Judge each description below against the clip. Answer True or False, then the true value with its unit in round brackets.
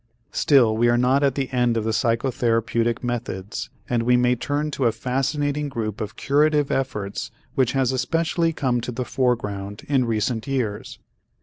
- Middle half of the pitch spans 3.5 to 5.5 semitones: False (3.0 semitones)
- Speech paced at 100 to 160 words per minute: False (170 wpm)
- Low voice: True (125 Hz)